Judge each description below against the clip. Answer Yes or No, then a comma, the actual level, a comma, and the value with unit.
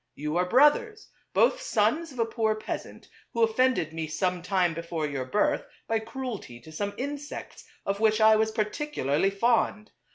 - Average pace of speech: Yes, average, 165 wpm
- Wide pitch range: Yes, wide, 6.2 semitones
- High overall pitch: Yes, high, 215 Hz